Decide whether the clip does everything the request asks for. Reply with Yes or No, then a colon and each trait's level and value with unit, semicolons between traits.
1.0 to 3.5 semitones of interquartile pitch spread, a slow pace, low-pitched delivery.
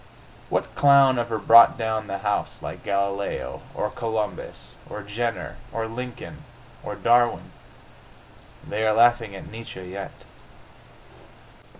Yes: average, 2.8 semitones; slow, 115 wpm; low, 110 Hz